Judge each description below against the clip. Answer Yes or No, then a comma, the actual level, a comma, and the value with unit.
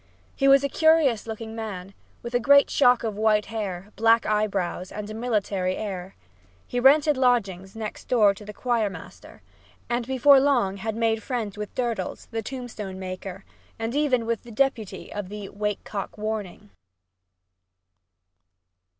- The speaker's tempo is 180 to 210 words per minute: No, average, 155 wpm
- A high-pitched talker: Yes, high, 220 Hz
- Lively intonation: No, average, 3.5 semitones